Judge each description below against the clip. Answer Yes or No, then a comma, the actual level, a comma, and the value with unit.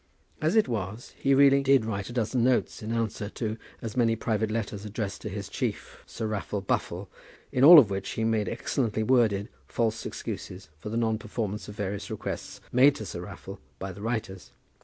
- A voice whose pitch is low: Yes, low, 110 Hz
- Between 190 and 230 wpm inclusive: Yes, average, 195 wpm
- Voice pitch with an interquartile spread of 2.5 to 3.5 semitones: Yes, average, 2.9 semitones